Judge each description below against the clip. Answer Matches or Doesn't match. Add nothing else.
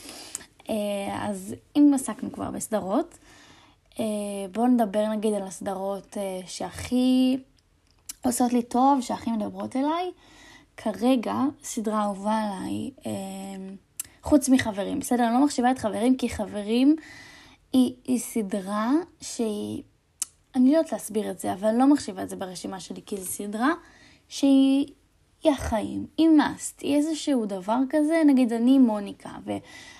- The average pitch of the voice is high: Matches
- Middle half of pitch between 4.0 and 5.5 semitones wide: Matches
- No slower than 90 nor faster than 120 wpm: Doesn't match